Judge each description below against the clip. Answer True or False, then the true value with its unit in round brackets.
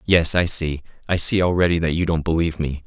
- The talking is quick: True (230 wpm)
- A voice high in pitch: False (85 Hz)